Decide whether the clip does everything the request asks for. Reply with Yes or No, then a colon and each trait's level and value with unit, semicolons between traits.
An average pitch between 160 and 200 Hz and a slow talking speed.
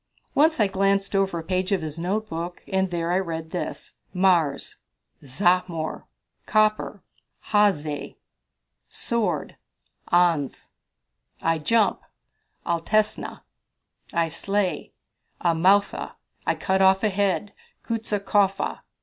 Yes: high, 190 Hz; slow, 100 wpm